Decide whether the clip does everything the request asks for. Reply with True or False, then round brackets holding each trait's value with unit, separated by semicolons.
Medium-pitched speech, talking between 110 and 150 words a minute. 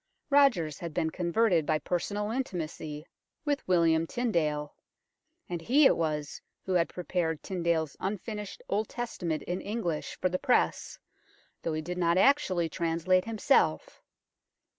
True (175 Hz; 140 wpm)